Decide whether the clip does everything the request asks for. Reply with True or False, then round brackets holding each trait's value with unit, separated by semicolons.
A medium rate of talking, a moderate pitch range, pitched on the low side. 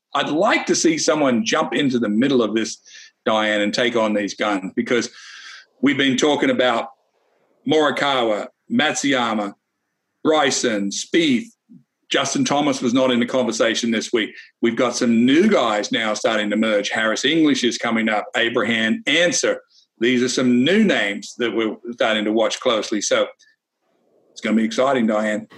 False (160 wpm; 6.5 semitones; 120 Hz)